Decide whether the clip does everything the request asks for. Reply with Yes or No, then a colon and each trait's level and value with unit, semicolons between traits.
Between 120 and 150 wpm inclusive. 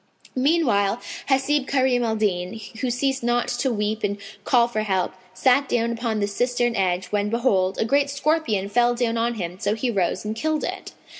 No: average, 190 wpm